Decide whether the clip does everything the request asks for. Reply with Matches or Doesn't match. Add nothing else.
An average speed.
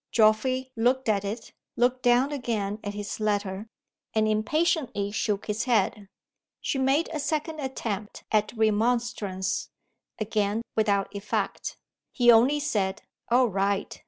Doesn't match